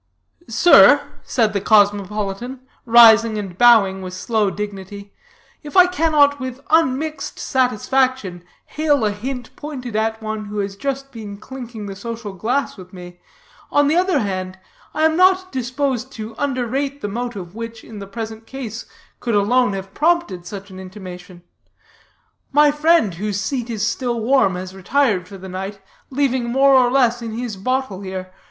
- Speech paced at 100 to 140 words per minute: No, average, 160 wpm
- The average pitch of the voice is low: No, high, 225 Hz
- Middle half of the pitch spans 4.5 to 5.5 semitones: Yes, average, 5.0 semitones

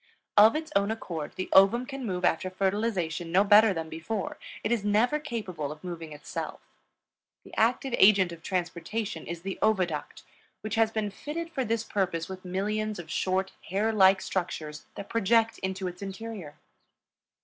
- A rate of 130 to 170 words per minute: Yes, average, 165 wpm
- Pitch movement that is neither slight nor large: Yes, average, 3.9 semitones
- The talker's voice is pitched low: No, high, 195 Hz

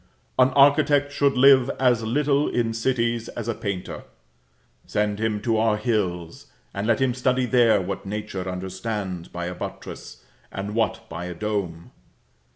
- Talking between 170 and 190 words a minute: No, average, 155 wpm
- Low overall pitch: Yes, low, 110 Hz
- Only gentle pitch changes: No, average, 4.3 semitones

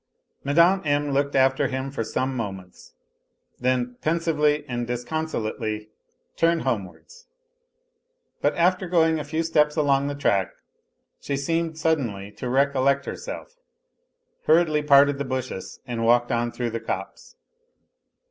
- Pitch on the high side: No, medium, 140 Hz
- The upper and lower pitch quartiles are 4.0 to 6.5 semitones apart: Yes, average, 4.6 semitones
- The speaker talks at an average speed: No, slow, 130 wpm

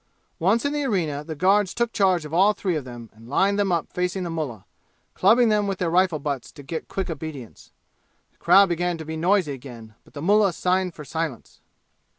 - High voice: No, medium, 175 Hz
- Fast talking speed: Yes, fast, 210 wpm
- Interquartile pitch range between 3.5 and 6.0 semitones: Yes, average, 4.6 semitones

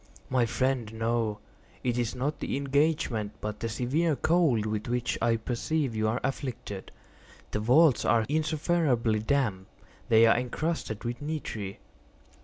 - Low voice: Yes, low, 120 Hz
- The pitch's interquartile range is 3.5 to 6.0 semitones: Yes, average, 4.3 semitones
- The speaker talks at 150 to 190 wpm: No, average, 140 wpm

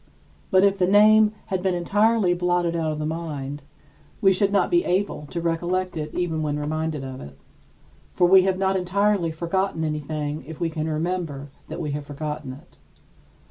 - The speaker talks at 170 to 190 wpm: Yes, average, 180 wpm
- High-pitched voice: No, medium, 170 Hz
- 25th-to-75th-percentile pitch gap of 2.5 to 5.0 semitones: Yes, average, 3.7 semitones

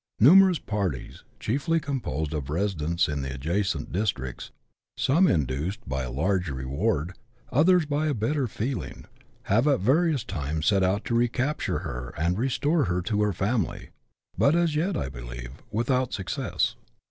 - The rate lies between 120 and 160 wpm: Yes, average, 150 wpm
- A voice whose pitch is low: Yes, low, 100 Hz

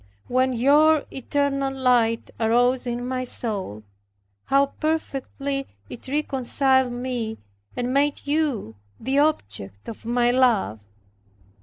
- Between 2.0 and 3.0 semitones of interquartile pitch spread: Yes, average, 2.7 semitones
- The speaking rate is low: Yes, slow, 110 wpm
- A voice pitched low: No, very high, 255 Hz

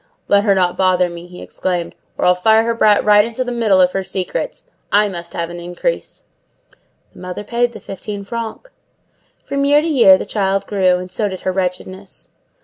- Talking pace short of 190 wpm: No, average, 200 wpm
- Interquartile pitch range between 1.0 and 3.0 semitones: No, average, 3.5 semitones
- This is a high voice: Yes, high, 195 Hz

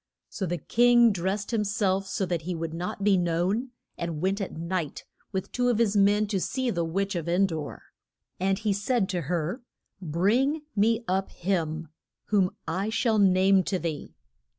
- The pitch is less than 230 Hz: Yes, high, 190 Hz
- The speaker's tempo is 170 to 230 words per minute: Yes, average, 180 wpm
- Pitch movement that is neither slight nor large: Yes, average, 3.4 semitones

